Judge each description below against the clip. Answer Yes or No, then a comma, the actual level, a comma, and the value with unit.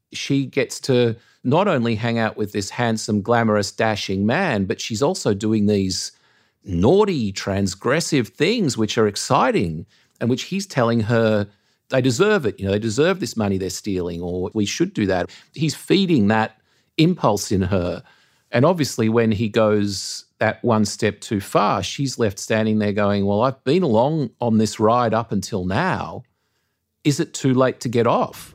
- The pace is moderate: Yes, average, 175 wpm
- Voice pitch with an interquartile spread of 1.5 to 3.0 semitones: No, average, 4.1 semitones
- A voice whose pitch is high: No, low, 110 Hz